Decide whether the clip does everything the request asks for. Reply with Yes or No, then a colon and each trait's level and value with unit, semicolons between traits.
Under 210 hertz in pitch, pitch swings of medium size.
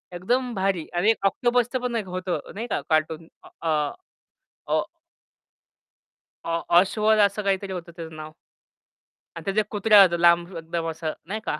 Yes: high, 190 Hz; average, 4.2 semitones